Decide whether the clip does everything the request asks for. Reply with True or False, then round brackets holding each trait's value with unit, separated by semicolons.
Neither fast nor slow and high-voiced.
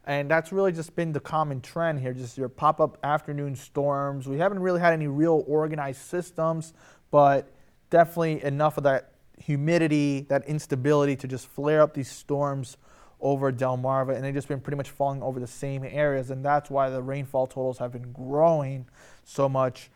False (185 wpm; 140 Hz)